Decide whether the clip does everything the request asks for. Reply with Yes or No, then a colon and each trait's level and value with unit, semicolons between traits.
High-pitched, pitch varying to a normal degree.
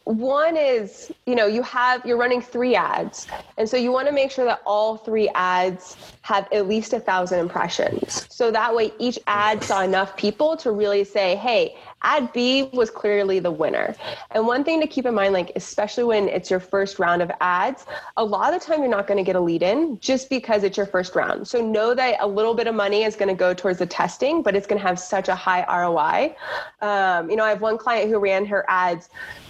Yes: high, 215 Hz; average, 4.3 semitones